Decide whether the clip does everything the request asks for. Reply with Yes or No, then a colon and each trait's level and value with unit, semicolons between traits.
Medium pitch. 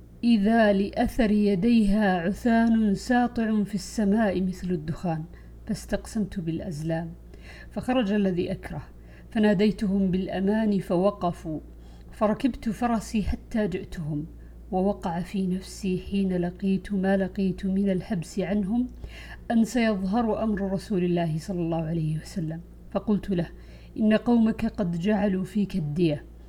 No: high, 195 Hz